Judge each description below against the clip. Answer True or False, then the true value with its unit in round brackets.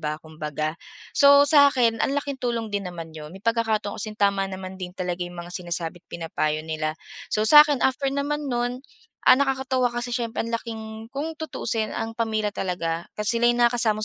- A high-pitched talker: True (220 Hz)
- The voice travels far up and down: True (5.7 semitones)